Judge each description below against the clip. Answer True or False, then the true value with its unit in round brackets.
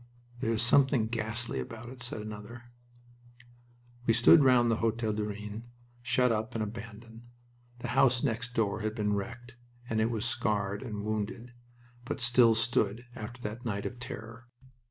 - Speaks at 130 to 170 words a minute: True (160 wpm)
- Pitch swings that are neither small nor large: False (2.0 semitones)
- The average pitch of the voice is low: True (115 Hz)